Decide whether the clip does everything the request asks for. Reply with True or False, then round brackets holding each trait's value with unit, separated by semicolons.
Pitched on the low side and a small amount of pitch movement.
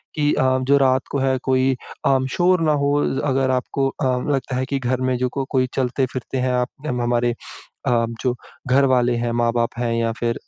True (130 Hz; 1.6 semitones)